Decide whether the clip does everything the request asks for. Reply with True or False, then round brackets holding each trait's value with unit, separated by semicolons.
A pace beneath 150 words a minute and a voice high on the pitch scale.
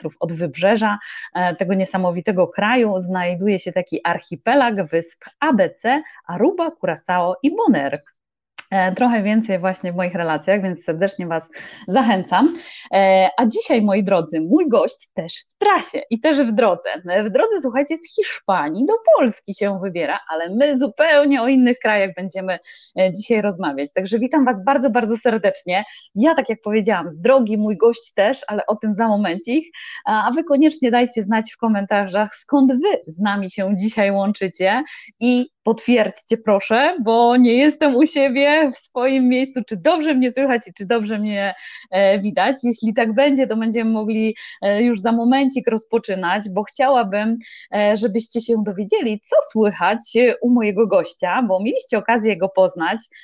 False (155 wpm; 225 Hz)